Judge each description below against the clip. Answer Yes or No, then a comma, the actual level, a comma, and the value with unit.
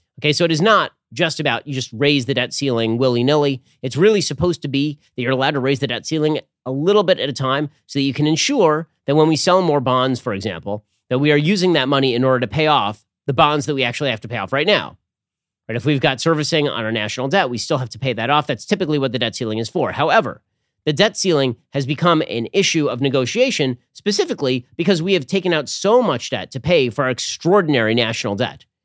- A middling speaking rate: No, fast, 245 wpm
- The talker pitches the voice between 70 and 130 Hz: No, medium, 140 Hz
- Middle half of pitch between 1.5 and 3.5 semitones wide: No, average, 4.0 semitones